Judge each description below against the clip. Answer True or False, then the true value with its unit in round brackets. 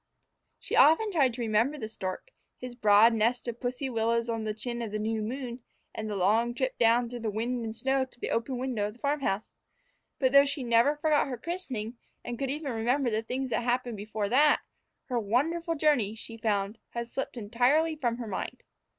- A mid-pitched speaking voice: False (240 Hz)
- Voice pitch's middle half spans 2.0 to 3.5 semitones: True (3.1 semitones)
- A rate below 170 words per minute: False (205 wpm)